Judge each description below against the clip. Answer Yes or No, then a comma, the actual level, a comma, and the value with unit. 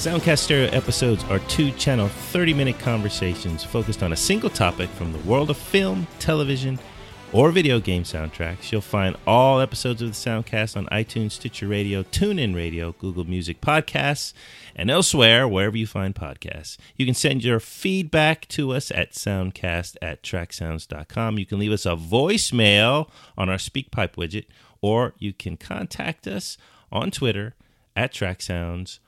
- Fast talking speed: No, average, 155 wpm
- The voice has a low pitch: Yes, low, 110 Hz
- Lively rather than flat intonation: Yes, wide, 5.9 semitones